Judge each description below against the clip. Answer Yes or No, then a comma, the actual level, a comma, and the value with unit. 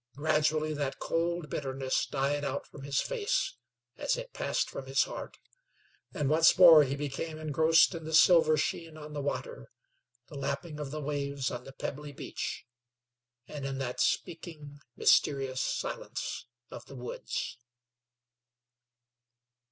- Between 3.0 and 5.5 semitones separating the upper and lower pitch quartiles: No, narrow, 2.6 semitones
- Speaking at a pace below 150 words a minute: Yes, average, 140 wpm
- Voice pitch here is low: No, medium, 150 Hz